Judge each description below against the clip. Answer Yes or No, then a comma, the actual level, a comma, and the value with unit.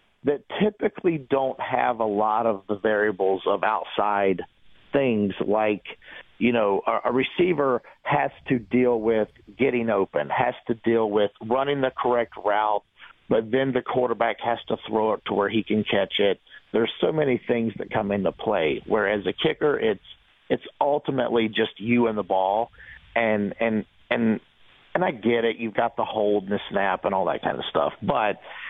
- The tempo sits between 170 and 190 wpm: Yes, average, 180 wpm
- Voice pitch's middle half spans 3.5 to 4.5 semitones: No, average, 2.9 semitones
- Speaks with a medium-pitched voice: No, low, 115 Hz